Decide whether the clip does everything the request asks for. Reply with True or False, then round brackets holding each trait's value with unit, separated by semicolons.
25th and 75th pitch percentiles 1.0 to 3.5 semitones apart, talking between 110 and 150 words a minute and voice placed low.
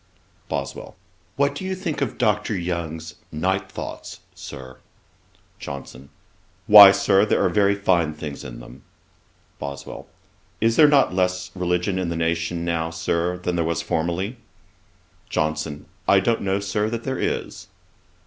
False (4.0 semitones; 145 wpm; 90 Hz)